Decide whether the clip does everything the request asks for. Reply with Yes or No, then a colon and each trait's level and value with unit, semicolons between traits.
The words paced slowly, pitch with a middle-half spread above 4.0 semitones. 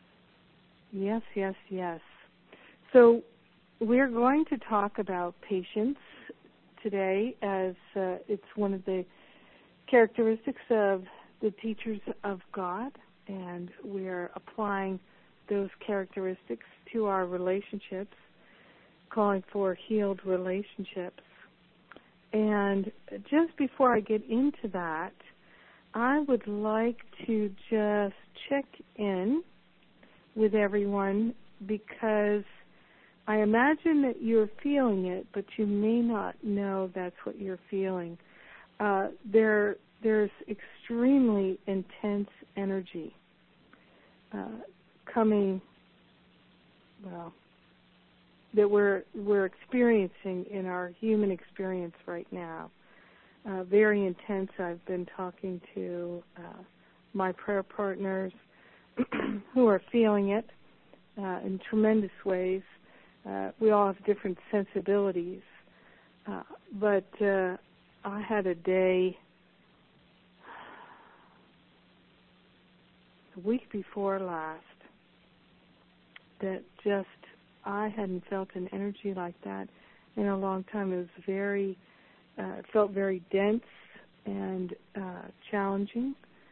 No: slow, 100 wpm; narrow, 2.5 semitones